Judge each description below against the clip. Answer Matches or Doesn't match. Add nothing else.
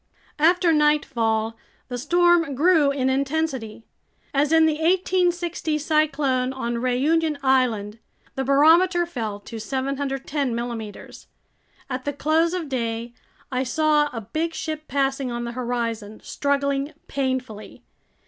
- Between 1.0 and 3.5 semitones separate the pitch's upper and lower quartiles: Doesn't match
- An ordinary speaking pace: Doesn't match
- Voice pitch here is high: Matches